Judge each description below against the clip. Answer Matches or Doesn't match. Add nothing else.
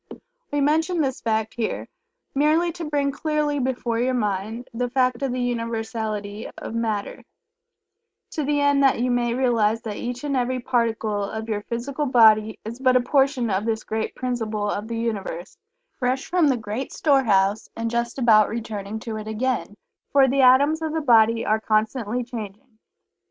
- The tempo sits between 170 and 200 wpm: Matches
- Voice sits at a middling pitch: Doesn't match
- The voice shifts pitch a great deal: Doesn't match